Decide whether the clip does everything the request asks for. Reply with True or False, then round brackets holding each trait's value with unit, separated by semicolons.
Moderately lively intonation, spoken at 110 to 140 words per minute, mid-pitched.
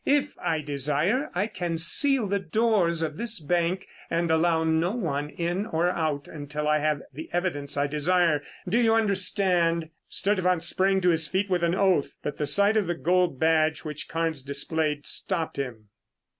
False (3.8 semitones; 175 wpm; 170 Hz)